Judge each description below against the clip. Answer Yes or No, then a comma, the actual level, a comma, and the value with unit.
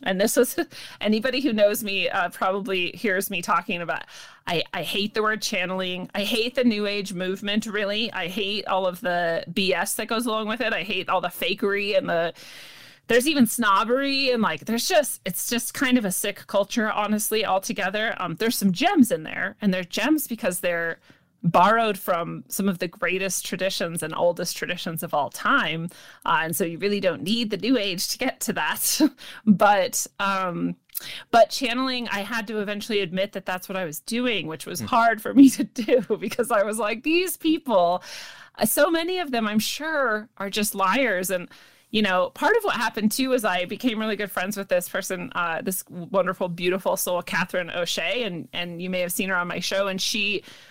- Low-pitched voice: No, high, 205 Hz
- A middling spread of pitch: Yes, average, 4.0 semitones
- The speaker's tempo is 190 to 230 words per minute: Yes, average, 200 wpm